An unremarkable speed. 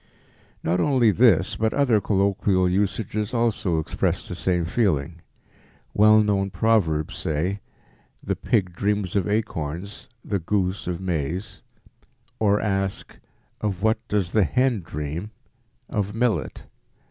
No: slow, 125 wpm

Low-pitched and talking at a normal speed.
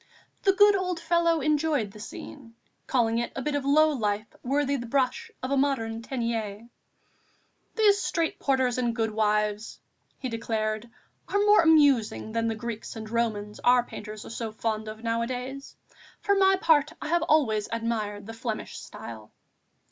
No: high, 235 Hz; average, 160 wpm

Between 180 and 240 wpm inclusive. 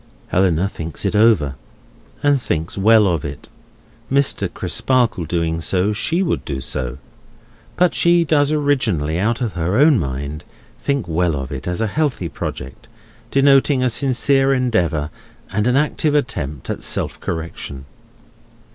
No: average, 145 wpm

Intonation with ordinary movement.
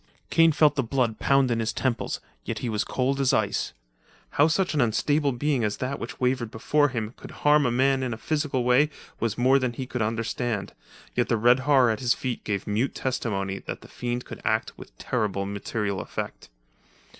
Yes: average, 3.5 semitones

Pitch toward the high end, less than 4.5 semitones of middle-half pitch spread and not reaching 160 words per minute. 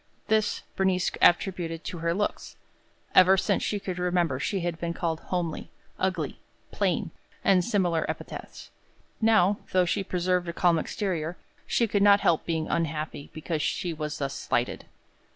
No: medium, 175 Hz; narrow, 2.6 semitones; average, 150 wpm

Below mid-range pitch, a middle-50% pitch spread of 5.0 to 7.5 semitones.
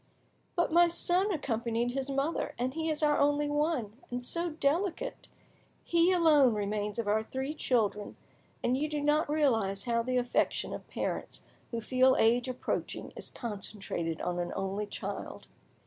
No: very high, 260 Hz; wide, 5.5 semitones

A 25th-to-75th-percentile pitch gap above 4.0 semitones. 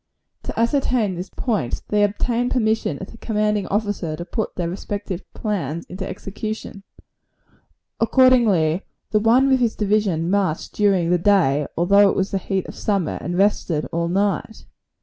No: average, 3.7 semitones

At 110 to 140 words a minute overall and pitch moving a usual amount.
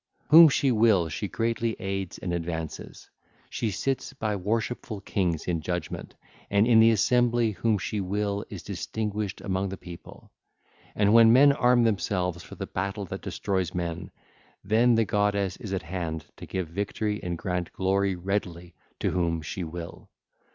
No: average, 160 wpm; average, 3.9 semitones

